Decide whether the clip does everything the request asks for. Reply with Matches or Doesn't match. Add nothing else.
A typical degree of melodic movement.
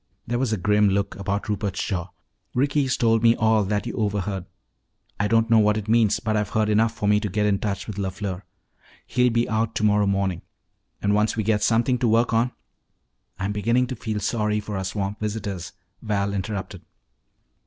Doesn't match